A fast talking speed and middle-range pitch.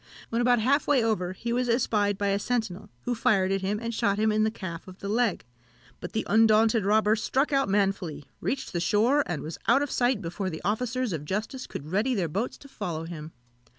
No: fast, 225 wpm; high, 215 Hz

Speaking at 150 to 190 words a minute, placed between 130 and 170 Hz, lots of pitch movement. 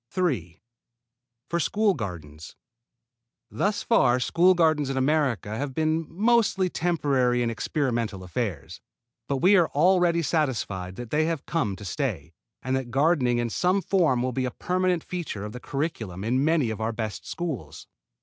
Yes: average, 160 wpm; low, 135 Hz; wide, 6.7 semitones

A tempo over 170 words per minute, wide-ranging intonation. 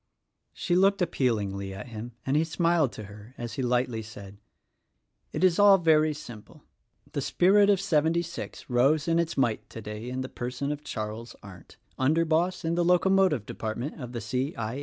Yes: average, 180 wpm; wide, 6.8 semitones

